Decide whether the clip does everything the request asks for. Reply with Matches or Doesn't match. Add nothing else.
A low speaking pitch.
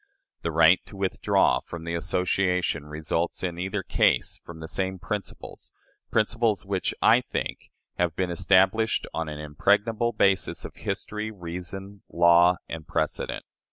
Matches